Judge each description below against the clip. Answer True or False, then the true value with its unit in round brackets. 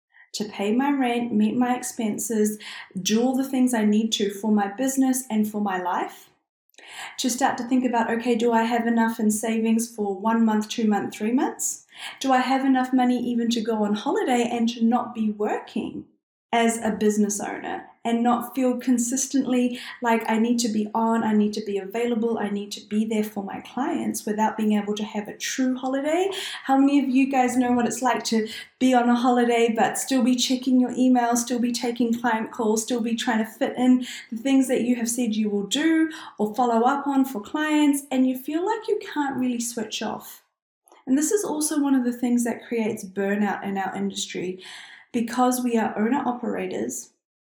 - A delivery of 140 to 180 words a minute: False (205 wpm)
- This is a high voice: True (235 Hz)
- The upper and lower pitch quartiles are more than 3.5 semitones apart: False (2.8 semitones)